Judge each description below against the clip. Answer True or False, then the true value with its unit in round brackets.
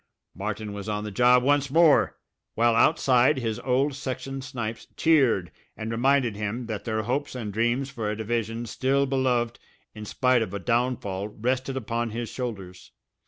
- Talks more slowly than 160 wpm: False (165 wpm)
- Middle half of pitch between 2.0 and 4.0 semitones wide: True (3.4 semitones)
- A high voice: False (120 Hz)